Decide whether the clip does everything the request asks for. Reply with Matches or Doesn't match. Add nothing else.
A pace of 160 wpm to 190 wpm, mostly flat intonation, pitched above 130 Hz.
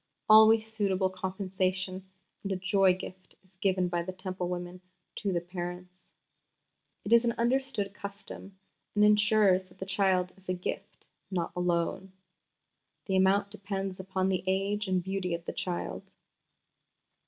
Doesn't match